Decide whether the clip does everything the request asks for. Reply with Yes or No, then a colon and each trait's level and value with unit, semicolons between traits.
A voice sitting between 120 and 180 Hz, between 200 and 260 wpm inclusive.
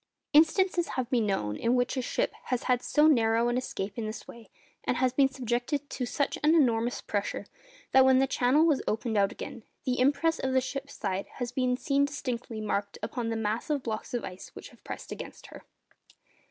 No: very high, 250 Hz; fast, 205 wpm